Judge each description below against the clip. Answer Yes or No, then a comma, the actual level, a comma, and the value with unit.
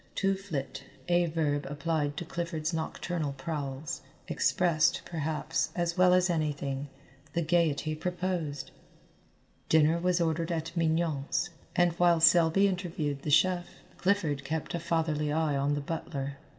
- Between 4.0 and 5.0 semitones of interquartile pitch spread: No, average, 2.9 semitones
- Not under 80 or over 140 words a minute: Yes, slow, 135 wpm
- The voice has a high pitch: No, medium, 160 Hz